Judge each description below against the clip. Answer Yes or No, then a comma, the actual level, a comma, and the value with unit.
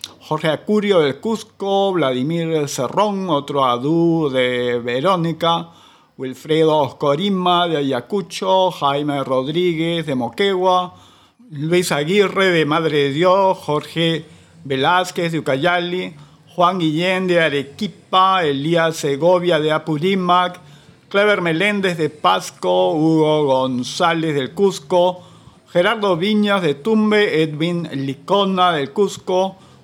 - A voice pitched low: No, medium, 170 Hz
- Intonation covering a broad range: No, average, 3.9 semitones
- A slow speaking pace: Yes, slow, 105 wpm